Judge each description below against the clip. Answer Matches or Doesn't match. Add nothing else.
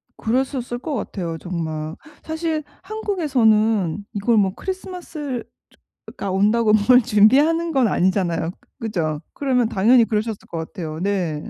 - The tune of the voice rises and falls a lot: Matches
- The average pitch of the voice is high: Matches